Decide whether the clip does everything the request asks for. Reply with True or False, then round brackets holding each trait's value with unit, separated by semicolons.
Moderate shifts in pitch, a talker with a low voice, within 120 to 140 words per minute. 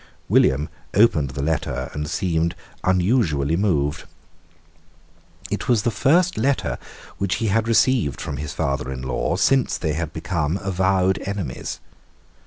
False (5.7 semitones; 90 Hz; 135 wpm)